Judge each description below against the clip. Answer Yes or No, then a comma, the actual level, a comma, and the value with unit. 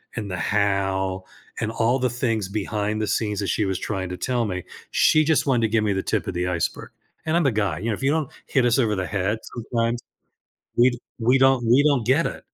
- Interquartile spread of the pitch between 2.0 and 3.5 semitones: No, average, 4.0 semitones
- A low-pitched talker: Yes, low, 110 Hz